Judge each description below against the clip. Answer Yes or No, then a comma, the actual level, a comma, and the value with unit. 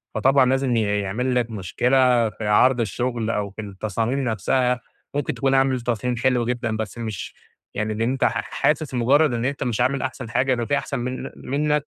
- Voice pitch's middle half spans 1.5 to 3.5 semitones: Yes, average, 2.9 semitones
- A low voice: Yes, low, 125 Hz